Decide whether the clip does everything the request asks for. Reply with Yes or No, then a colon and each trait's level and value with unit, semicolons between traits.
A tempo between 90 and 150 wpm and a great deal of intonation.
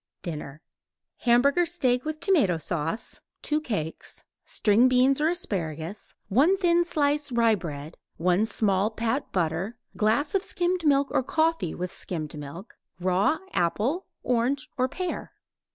Yes: slow, 135 wpm; wide, 8.9 semitones